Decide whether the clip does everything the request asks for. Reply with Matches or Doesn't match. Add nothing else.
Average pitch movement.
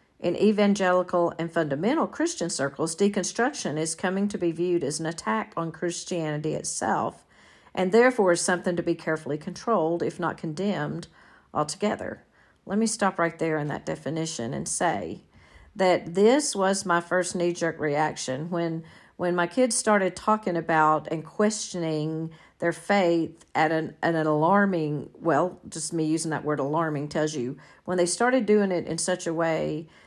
Matches